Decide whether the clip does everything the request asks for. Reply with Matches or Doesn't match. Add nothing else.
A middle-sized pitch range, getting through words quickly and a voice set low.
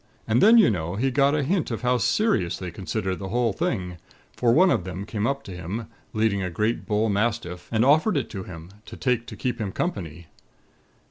Doesn't match